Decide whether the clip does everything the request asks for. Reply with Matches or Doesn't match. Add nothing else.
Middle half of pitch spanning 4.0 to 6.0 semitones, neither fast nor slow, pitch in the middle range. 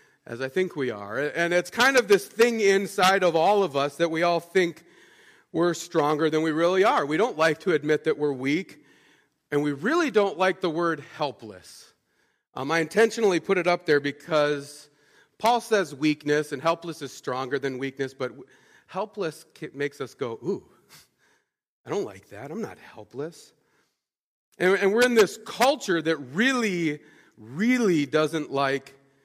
Matches